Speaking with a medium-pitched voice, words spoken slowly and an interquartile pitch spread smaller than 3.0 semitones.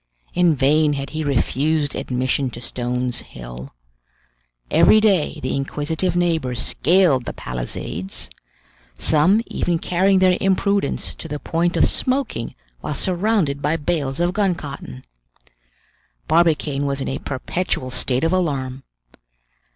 No: medium, 150 Hz; slow, 130 wpm; average, 5.0 semitones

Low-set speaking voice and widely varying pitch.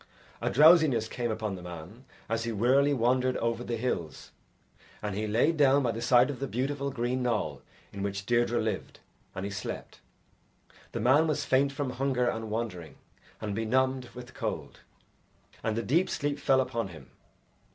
No: low, 120 Hz; average, 3.5 semitones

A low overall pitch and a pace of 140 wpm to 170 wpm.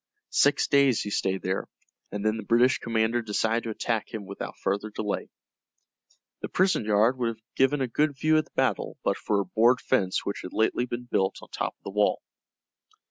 No: low, 110 Hz; average, 200 wpm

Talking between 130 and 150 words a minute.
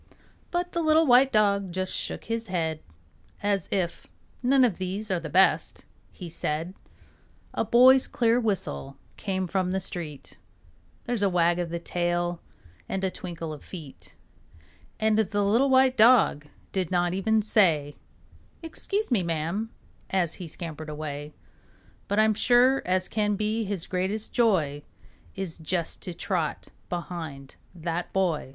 Yes: average, 145 wpm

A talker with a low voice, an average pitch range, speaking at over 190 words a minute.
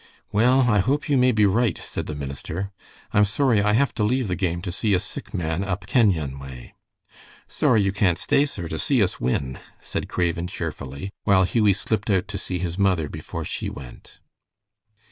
Yes: low, 100 Hz; average, 4.3 semitones; average, 200 wpm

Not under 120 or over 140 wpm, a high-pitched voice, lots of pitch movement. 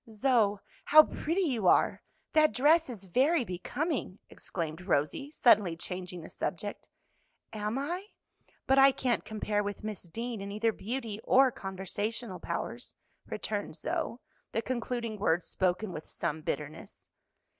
Yes: slow, 135 wpm; high, 215 Hz; wide, 5.8 semitones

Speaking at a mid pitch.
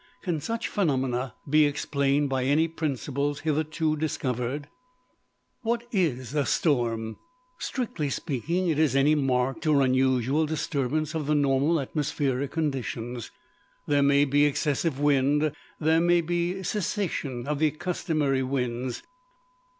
Yes: medium, 145 Hz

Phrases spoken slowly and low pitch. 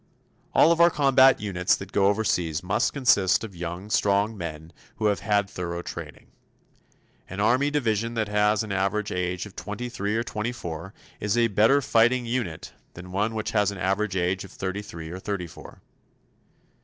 No: average, 180 wpm; low, 105 Hz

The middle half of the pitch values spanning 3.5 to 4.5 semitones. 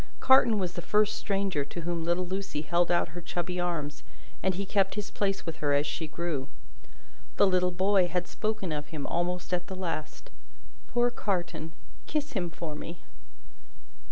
No: average, 2.9 semitones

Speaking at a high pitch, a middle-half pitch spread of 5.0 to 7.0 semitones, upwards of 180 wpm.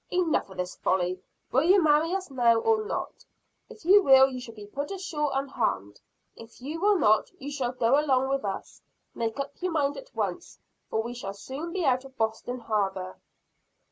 Yes: very high, 265 Hz; wide, 5.6 semitones; average, 195 wpm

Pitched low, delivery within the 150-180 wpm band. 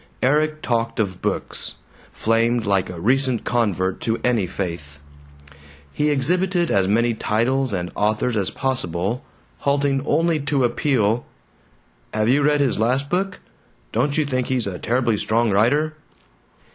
No: low, 120 Hz; average, 140 wpm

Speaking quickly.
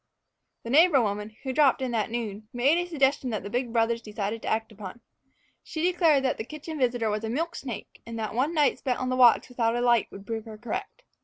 Yes: fast, 235 wpm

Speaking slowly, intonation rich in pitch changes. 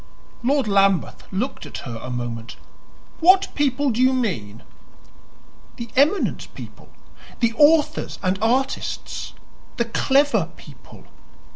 Yes: slow, 115 wpm; wide, 7.2 semitones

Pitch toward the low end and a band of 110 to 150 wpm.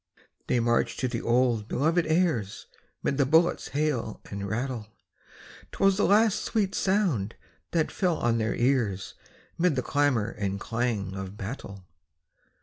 Yes: low, 125 Hz; average, 145 wpm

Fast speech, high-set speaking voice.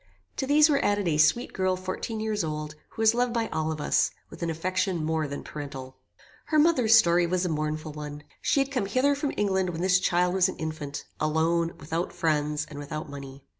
No: fast, 210 wpm; medium, 170 Hz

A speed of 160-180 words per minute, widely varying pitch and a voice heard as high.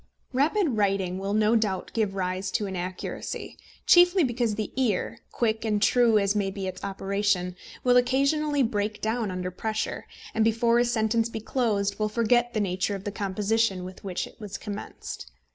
No: average, 175 wpm; average, 3.2 semitones; high, 215 Hz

